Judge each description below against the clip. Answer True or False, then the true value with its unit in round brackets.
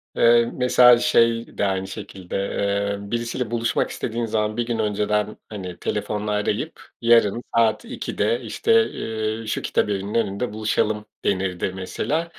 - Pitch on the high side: False (110 Hz)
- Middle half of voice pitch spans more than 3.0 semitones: False (2.6 semitones)